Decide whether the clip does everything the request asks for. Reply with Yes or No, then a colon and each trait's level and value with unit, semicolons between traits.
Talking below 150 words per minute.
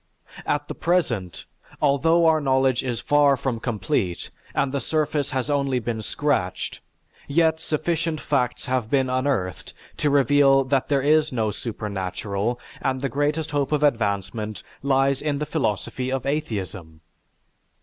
Yes: average, 140 wpm